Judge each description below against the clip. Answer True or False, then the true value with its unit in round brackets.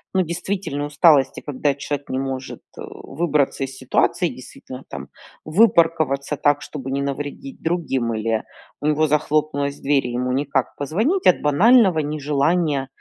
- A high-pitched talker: False (145 Hz)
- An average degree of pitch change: True (3.1 semitones)